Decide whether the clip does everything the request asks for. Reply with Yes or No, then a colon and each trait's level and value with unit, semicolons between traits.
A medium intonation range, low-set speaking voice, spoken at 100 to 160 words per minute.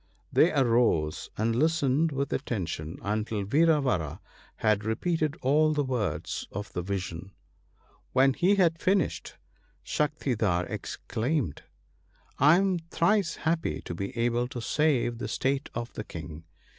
No: wide, 7.2 semitones; low, 125 Hz; slow, 135 wpm